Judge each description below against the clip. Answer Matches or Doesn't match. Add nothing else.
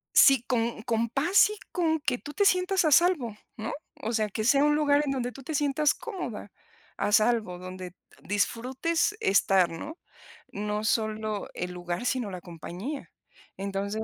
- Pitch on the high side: Matches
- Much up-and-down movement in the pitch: Matches